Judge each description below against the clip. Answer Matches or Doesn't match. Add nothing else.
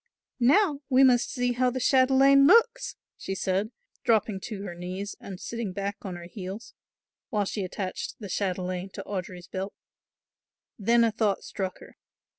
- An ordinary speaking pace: Matches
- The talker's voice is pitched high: Matches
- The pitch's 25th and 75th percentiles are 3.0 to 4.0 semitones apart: Doesn't match